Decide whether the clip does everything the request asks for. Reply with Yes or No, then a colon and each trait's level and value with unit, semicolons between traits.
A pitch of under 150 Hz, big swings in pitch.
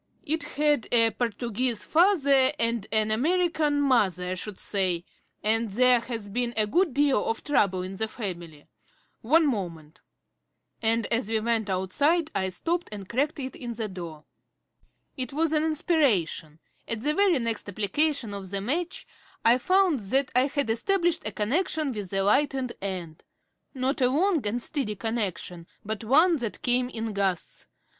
No: high, 235 Hz; wide, 6.2 semitones